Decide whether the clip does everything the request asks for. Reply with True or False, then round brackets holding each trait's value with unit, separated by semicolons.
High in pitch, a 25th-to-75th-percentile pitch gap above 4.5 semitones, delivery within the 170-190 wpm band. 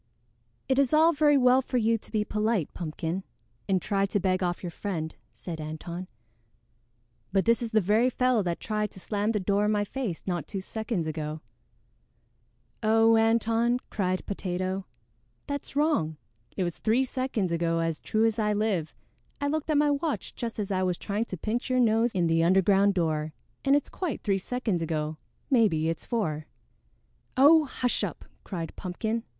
True (210 Hz; 5.1 semitones; 180 wpm)